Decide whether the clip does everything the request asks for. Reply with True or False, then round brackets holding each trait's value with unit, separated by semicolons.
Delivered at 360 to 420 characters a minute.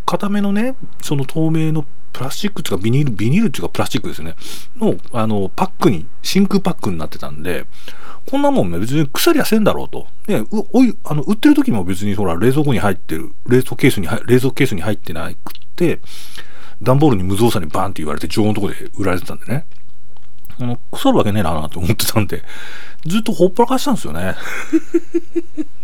True (415 characters per minute)